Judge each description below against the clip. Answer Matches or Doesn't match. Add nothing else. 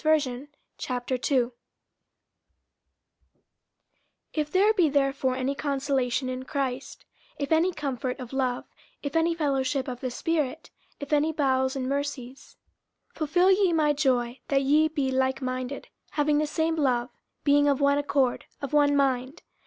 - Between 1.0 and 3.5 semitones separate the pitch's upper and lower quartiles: Matches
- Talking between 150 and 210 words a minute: Doesn't match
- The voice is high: Matches